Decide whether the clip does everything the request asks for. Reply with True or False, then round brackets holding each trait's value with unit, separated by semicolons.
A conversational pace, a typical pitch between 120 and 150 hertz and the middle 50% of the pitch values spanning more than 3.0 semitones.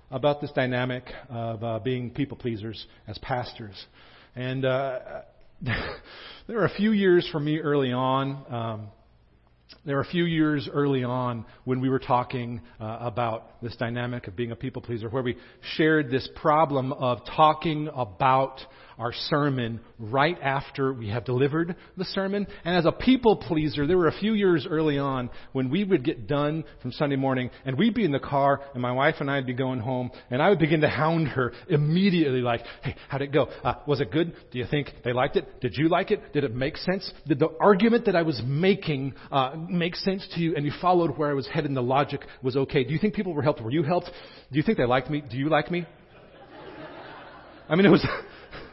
False (210 wpm; 140 Hz; 4.4 semitones)